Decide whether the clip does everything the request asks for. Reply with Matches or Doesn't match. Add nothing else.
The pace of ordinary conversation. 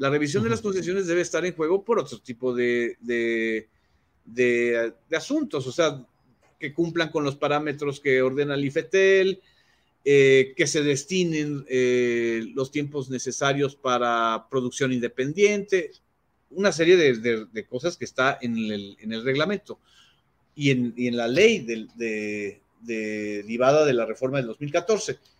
Matches